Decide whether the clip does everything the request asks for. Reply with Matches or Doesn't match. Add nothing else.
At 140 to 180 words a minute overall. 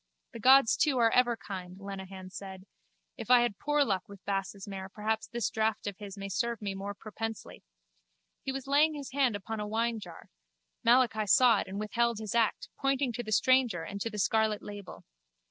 Doesn't match